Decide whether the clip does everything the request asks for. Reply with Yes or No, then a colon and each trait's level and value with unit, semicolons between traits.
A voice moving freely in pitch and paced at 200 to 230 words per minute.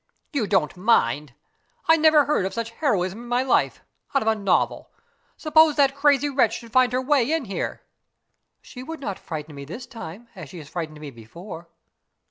No: wide, 8.2 semitones; average, 185 wpm